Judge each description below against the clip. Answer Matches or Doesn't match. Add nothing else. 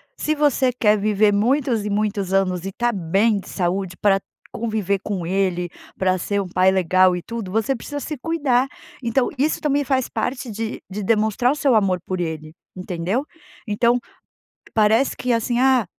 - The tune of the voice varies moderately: Matches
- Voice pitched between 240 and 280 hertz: Doesn't match